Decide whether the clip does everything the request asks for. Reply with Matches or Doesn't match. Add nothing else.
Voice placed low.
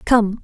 Doesn't match